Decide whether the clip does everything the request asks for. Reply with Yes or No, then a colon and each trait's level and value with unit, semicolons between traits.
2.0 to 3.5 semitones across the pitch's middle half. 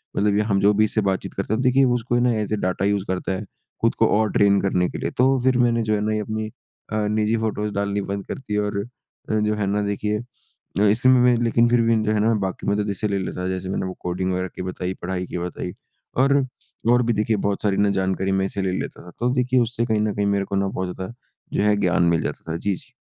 Yes: average, 2.9 semitones